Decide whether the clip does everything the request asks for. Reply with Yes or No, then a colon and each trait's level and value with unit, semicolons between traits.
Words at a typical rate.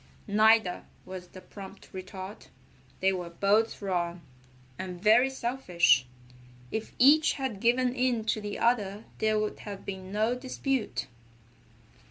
No: slow, 130 wpm